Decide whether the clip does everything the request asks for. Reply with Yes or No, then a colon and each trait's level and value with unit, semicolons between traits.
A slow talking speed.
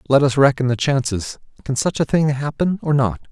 No: average, 200 wpm